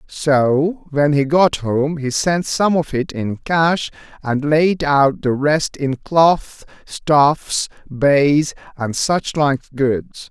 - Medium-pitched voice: Yes, medium, 145 Hz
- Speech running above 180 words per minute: No, average, 145 wpm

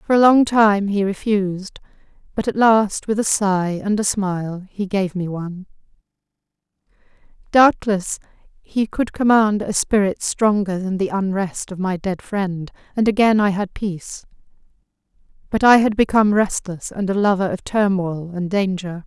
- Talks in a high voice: Yes, high, 200 Hz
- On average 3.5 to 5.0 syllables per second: Yes, 4.6 syllables/s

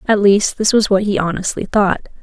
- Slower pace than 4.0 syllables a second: No, 5.4 syllables/s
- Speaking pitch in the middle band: No, high, 200 Hz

